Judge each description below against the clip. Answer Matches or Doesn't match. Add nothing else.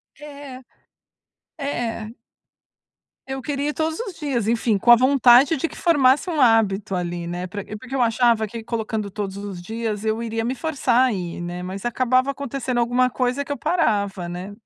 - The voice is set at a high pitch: Matches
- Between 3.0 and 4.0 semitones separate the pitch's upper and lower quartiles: Doesn't match